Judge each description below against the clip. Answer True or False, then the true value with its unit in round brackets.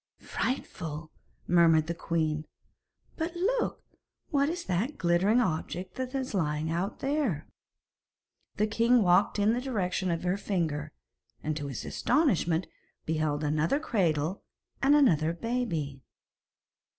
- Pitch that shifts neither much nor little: False (7.9 semitones)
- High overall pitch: False (180 Hz)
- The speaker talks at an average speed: False (125 wpm)